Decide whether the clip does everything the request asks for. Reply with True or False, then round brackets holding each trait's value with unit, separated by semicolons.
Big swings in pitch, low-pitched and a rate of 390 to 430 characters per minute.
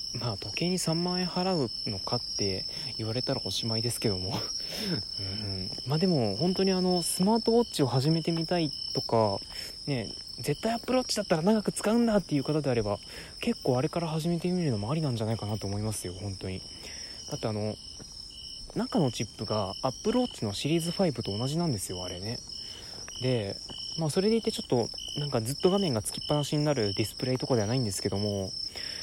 True (8.2 semitones; 130 Hz; 410 characters per minute)